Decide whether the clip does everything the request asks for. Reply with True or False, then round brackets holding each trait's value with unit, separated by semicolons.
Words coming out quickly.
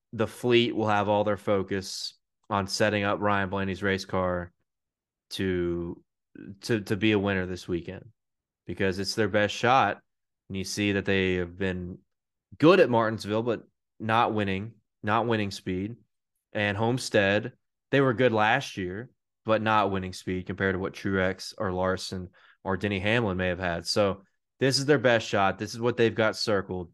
False (175 wpm)